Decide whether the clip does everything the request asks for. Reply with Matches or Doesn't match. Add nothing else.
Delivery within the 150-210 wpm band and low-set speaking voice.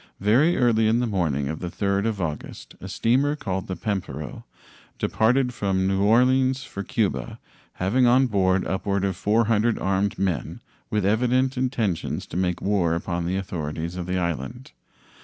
Matches